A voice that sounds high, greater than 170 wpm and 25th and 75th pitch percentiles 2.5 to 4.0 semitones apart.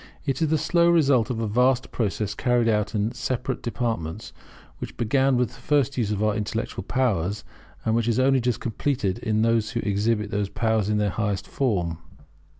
No: low, 115 Hz; average, 190 wpm; average, 3.3 semitones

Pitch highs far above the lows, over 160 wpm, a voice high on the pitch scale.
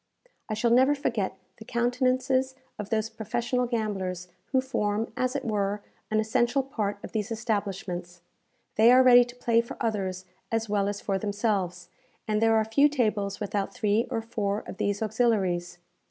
No: average, 3.0 semitones; average, 170 wpm; high, 220 Hz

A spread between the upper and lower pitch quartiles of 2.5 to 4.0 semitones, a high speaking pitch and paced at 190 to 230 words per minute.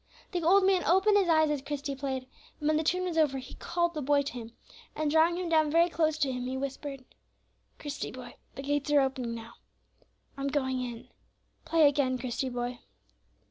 Yes: average, 3.6 semitones; very high, 290 Hz; average, 200 wpm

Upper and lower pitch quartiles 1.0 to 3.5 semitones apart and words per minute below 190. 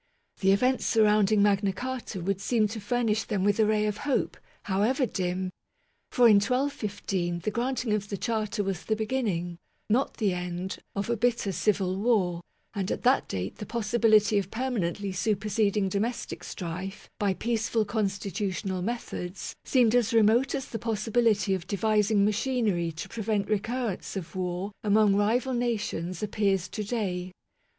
Yes: average, 3.0 semitones; average, 155 wpm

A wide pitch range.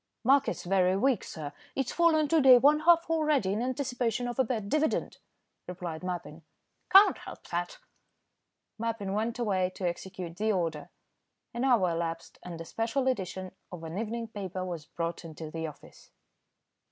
Yes: wide, 6.5 semitones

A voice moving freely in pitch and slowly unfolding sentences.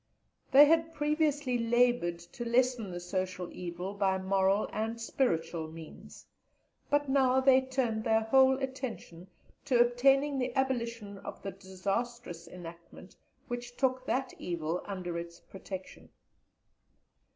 Yes: wide, 6.0 semitones; slow, 125 wpm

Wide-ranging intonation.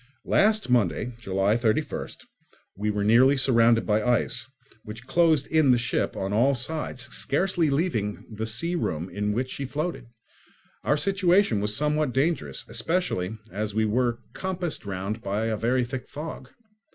Yes: wide, 6.1 semitones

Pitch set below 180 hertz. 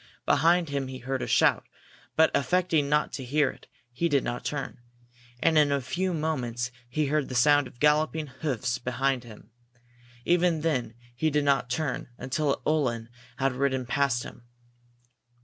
Yes: medium, 140 Hz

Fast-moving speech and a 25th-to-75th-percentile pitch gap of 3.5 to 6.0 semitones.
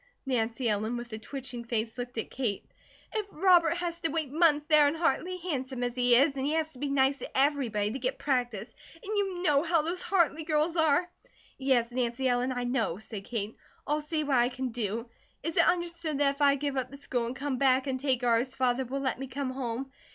Yes: fast, 230 wpm; average, 3.9 semitones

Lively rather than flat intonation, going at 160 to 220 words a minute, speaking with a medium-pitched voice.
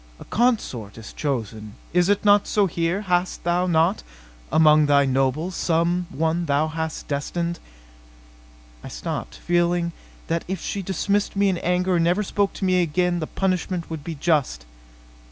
No: average, 4.0 semitones; average, 165 wpm; medium, 170 Hz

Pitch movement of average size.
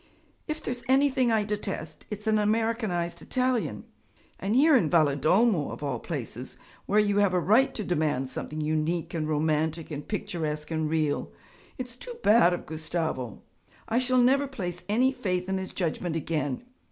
No: wide, 6.5 semitones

